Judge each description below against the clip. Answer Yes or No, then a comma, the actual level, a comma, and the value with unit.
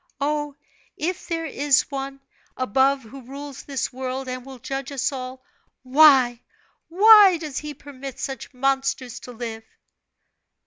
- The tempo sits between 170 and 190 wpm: No, slow, 135 wpm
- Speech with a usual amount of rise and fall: No, narrow, 2.1 semitones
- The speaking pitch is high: Yes, very high, 270 Hz